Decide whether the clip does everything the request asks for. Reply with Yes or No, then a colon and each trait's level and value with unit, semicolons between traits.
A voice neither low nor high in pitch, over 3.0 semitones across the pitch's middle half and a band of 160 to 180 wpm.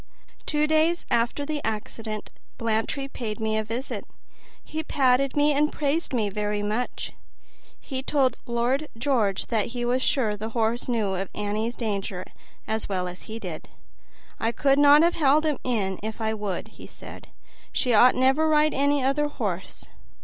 No: high, 240 Hz; average, 4.8 semitones; average, 170 wpm